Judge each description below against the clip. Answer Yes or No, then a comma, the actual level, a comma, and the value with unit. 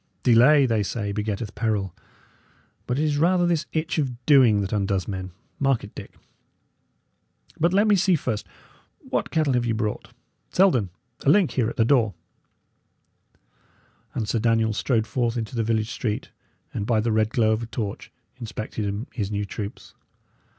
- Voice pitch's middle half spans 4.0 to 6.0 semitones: Yes, average, 4.3 semitones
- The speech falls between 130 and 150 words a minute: No, average, 165 wpm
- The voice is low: Yes, low, 115 Hz